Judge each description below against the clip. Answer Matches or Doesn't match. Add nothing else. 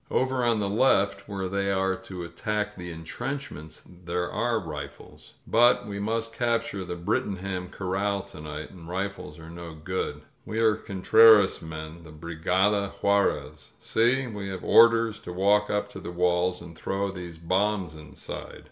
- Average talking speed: Matches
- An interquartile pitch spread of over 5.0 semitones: Doesn't match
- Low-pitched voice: Matches